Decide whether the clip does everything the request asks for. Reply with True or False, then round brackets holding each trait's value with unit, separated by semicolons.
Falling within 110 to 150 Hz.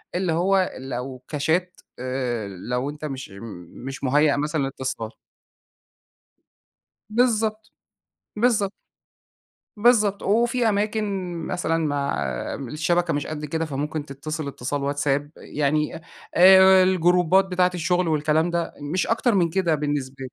False (160 Hz)